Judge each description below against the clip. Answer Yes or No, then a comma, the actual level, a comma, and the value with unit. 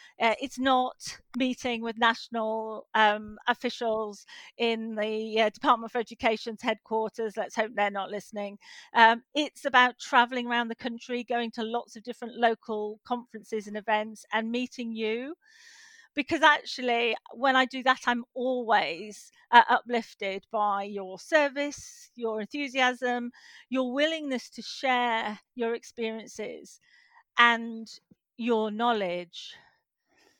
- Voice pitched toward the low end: No, high, 235 Hz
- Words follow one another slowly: Yes, slow, 125 wpm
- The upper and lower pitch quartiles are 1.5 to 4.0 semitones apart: Yes, narrow, 2.6 semitones